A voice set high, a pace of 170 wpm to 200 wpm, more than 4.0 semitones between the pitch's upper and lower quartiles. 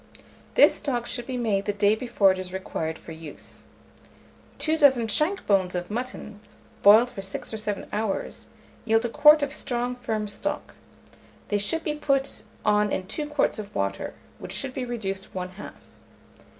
Yes: high, 215 Hz; average, 175 wpm; average, 4.5 semitones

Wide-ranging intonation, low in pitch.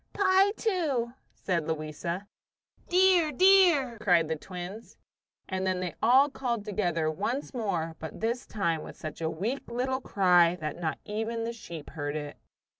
No: wide, 7.6 semitones; high, 205 Hz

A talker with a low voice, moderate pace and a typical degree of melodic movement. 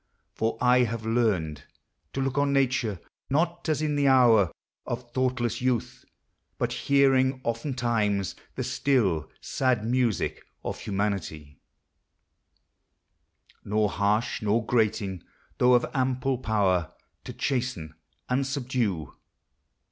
No: low, 120 Hz; slow, 110 wpm; average, 4.0 semitones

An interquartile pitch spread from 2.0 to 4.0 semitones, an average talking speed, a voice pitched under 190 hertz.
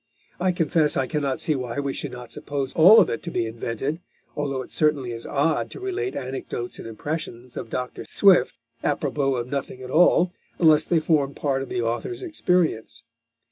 No: average, 4.4 semitones; average, 190 wpm; medium, 140 Hz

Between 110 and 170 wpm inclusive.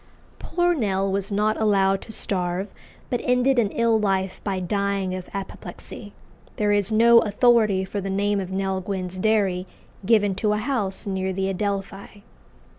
Yes: average, 160 wpm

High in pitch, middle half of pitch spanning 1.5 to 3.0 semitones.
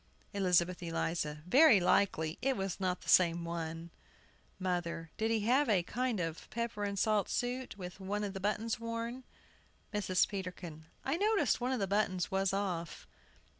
No: high, 195 Hz; average, 4.7 semitones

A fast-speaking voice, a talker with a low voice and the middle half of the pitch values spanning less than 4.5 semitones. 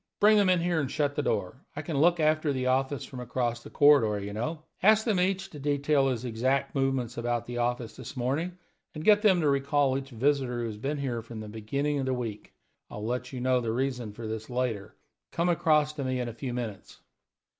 Yes: fast, 230 wpm; low, 130 Hz; average, 3.8 semitones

